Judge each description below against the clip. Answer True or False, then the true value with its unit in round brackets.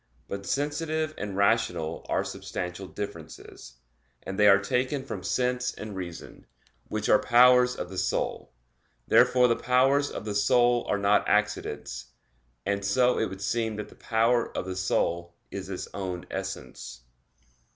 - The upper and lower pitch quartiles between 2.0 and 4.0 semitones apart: False (4.5 semitones)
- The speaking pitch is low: True (105 Hz)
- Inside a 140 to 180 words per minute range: True (150 wpm)